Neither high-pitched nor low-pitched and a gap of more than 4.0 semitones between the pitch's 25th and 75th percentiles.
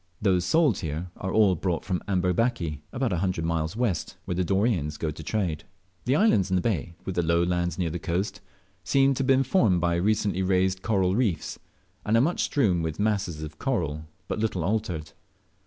No: very low, 95 Hz; average, 4.4 semitones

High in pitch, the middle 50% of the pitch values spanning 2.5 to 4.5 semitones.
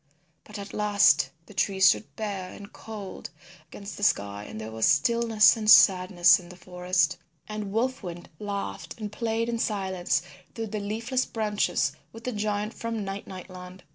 Yes: high, 200 Hz; average, 3.0 semitones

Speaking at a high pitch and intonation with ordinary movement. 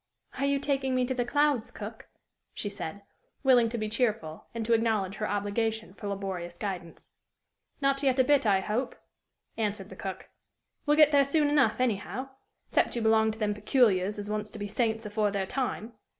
Yes: high, 220 Hz; average, 4.2 semitones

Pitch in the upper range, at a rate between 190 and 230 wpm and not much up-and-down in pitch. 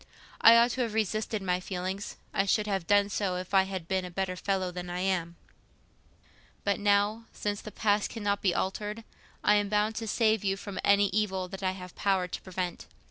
Yes: high, 195 Hz; fast, 205 wpm; narrow, 2.0 semitones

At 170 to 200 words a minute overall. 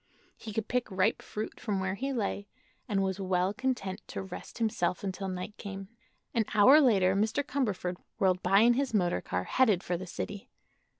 Yes: average, 185 wpm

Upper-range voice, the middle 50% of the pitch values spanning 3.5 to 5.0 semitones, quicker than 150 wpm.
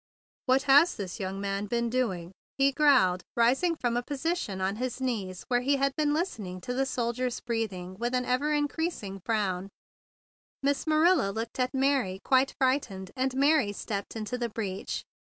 No: high, 245 Hz; wide, 5.6 semitones; average, 175 wpm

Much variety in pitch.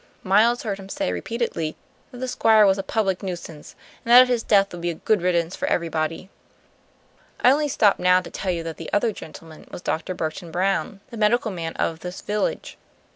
No: average, 4.4 semitones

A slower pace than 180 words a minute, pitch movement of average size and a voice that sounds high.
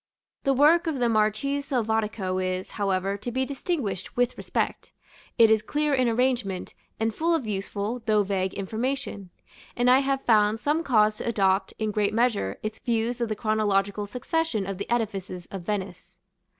Yes: average, 165 wpm; average, 3.9 semitones; high, 220 Hz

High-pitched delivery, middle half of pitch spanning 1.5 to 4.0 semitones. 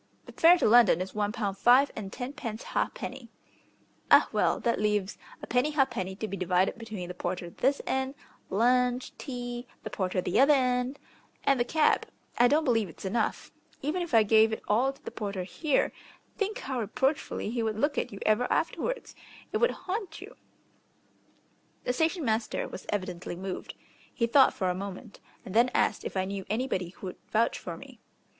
No: high, 235 Hz; average, 5.2 semitones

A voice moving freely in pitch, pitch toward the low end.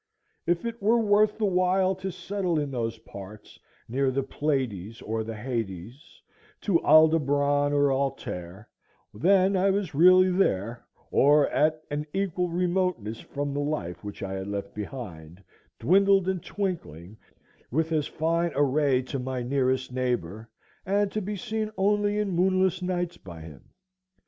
No: wide, 8.1 semitones; medium, 145 Hz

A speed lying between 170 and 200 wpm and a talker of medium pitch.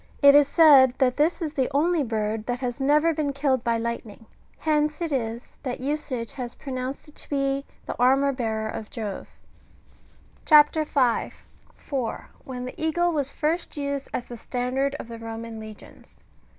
No: average, 175 wpm; very high, 270 Hz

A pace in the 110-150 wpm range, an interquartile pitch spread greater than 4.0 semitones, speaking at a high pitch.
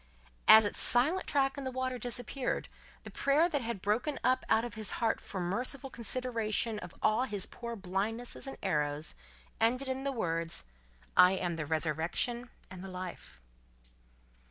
No: average, 165 wpm; wide, 5.5 semitones; high, 225 Hz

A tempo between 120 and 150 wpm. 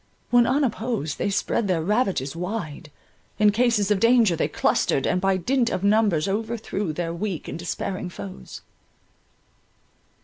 Yes: average, 140 wpm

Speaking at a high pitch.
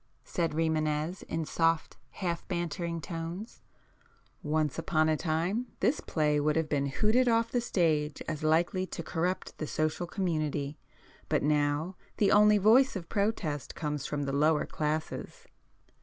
No: medium, 165 Hz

